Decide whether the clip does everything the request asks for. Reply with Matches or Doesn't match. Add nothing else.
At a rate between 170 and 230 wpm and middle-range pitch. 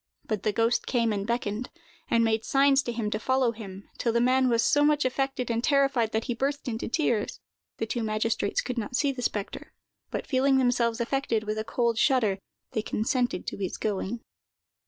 Doesn't match